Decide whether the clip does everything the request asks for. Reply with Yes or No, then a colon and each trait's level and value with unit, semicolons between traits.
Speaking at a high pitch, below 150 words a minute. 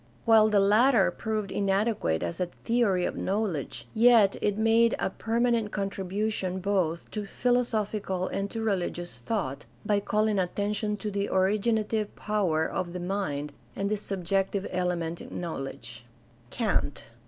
Yes: high, 200 Hz; average, 140 wpm